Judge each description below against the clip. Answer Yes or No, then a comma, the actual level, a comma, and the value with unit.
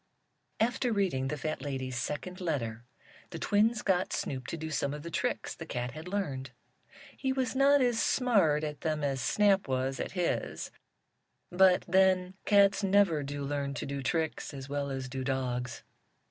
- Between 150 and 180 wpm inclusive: Yes, average, 175 wpm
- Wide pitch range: Yes, wide, 6.3 semitones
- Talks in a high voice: No, medium, 155 Hz